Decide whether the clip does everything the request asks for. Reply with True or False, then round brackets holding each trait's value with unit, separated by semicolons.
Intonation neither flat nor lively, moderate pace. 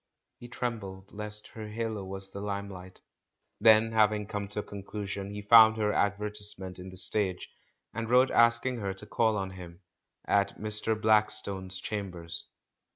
False (2.1 semitones; 160 wpm)